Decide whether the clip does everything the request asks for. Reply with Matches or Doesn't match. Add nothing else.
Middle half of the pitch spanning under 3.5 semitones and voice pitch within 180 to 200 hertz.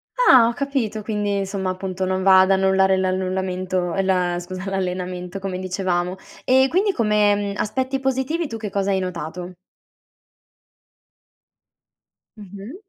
Matches